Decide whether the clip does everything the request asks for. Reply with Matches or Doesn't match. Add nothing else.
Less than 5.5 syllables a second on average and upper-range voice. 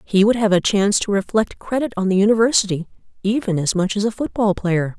Doesn't match